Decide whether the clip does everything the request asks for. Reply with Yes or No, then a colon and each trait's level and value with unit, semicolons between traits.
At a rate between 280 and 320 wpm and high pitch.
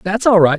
Yes: fast, 305 wpm; high, 195 Hz